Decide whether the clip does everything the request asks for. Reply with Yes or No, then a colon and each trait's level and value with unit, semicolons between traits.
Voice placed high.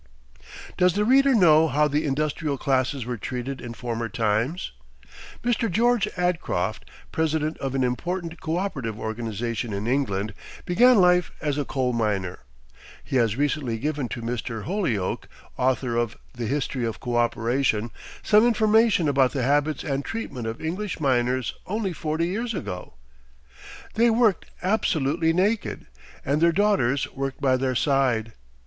No: medium, 140 Hz